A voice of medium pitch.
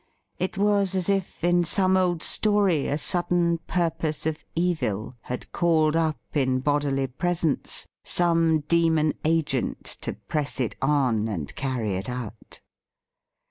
Yes: medium, 160 Hz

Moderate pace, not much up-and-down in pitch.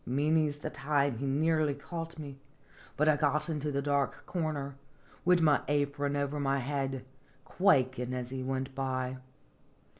Yes: average, 150 wpm; narrow, 2.2 semitones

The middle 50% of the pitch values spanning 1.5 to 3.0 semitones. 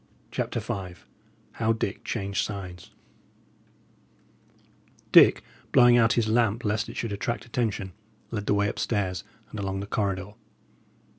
Yes: narrow, 2.6 semitones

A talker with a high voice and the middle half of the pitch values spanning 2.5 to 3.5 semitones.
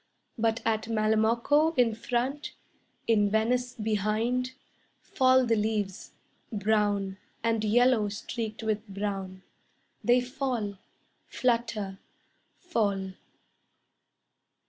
Yes: high, 220 Hz; average, 2.8 semitones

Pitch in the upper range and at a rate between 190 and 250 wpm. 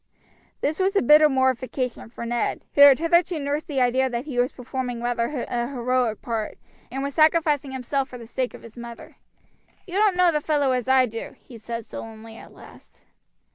Yes: very high, 260 Hz; average, 195 wpm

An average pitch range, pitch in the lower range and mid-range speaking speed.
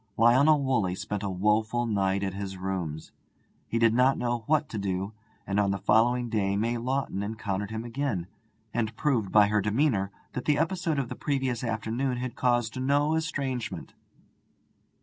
Yes: average, 4.5 semitones; low, 115 Hz; average, 170 wpm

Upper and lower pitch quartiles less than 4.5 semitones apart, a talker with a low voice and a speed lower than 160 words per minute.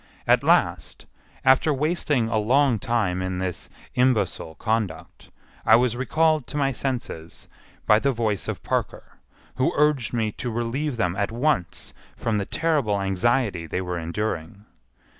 No: wide, 5.5 semitones; low, 115 Hz; average, 145 wpm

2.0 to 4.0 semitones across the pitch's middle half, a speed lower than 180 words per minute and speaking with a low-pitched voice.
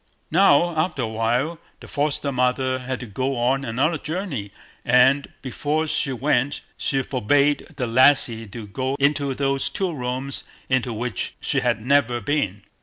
Yes: average, 2.9 semitones; average, 155 wpm; low, 130 Hz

